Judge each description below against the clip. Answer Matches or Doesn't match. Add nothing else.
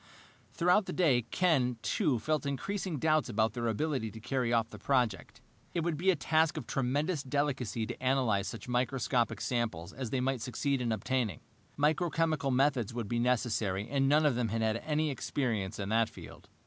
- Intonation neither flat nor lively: Matches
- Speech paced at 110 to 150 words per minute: Doesn't match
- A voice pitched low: Matches